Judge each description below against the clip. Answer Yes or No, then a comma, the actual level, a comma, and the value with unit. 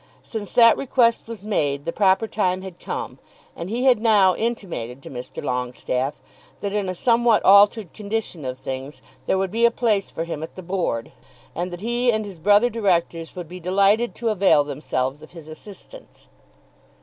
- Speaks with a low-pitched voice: No, high, 190 Hz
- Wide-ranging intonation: Yes, wide, 5.7 semitones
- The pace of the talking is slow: No, average, 185 wpm